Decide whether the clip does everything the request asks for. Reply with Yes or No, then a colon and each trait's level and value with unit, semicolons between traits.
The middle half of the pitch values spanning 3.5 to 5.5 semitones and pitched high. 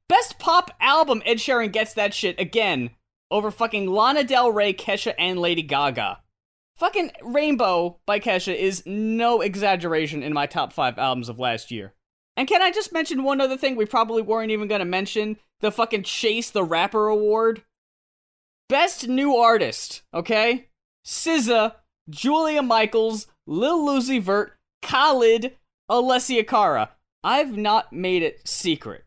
Yes: average, 4.7 semitones; high, 220 Hz